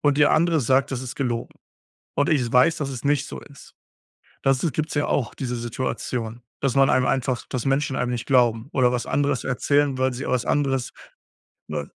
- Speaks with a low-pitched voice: Yes, low, 130 Hz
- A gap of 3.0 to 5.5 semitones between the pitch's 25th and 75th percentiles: No, narrow, 2.5 semitones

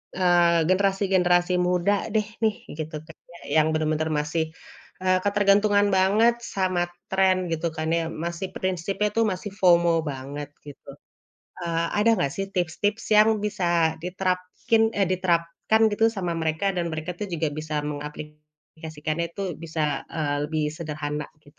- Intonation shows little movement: No, average, 3.8 semitones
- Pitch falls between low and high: Yes, medium, 175 Hz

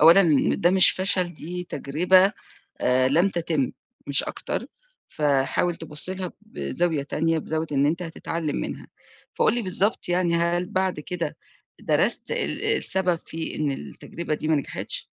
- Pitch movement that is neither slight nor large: Yes, average, 3.2 semitones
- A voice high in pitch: No, medium, 170 Hz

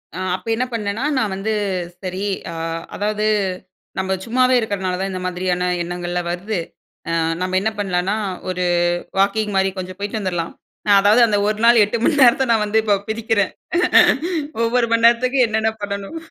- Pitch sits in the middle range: No, high, 205 Hz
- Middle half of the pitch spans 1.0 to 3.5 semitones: Yes, average, 3.2 semitones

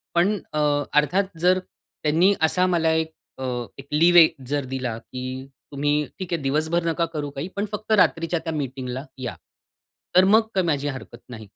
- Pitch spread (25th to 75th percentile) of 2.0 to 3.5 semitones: No, average, 4.1 semitones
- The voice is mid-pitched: Yes, medium, 160 Hz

